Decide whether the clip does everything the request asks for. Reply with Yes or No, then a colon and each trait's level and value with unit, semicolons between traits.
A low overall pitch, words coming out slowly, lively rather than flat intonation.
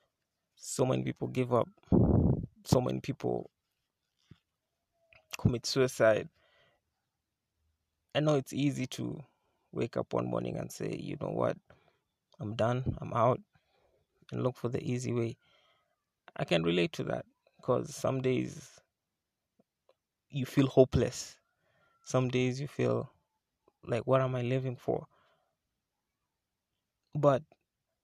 Yes: low, 120 Hz; slow, 120 wpm; wide, 7.0 semitones